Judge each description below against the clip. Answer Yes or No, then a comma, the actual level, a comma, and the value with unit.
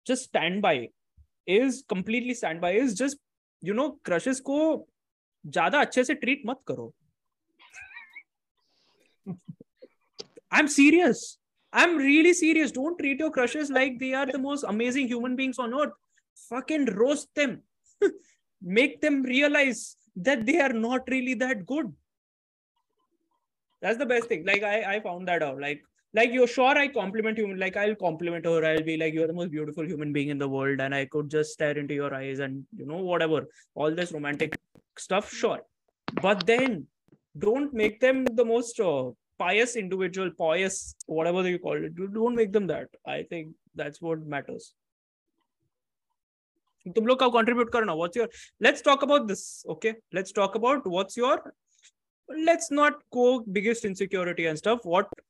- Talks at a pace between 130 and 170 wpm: Yes, average, 150 wpm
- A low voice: No, high, 235 Hz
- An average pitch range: No, wide, 8.0 semitones